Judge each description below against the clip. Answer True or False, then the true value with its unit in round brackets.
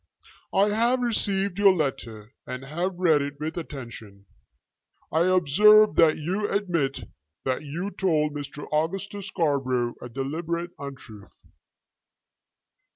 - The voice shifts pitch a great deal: True (5.9 semitones)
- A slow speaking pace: True (115 wpm)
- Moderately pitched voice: True (160 Hz)